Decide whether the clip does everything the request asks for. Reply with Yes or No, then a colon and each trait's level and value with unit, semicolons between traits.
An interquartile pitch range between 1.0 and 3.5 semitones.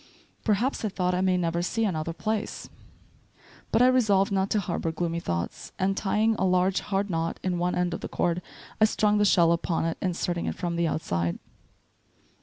Yes: average, 3.2 semitones